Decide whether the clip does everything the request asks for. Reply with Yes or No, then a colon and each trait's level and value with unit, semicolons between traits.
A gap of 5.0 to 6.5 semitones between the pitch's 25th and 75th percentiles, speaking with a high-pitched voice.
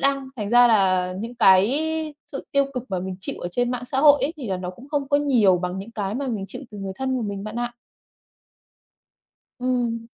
Yes: average, 5.3 semitones; high, 235 Hz